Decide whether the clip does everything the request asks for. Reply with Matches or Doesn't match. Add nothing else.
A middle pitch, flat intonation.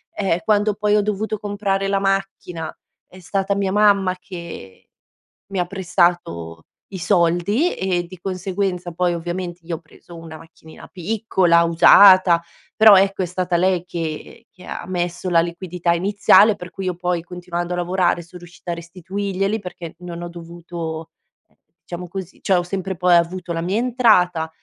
Matches